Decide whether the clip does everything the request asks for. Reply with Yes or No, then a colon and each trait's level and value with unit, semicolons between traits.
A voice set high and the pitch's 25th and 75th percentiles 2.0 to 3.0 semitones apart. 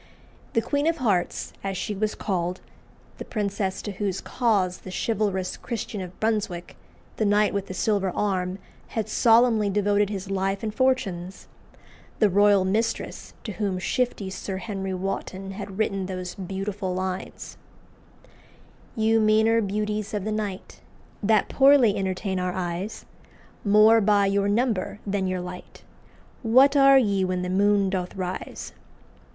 Yes: high, 200 Hz; narrow, 2.4 semitones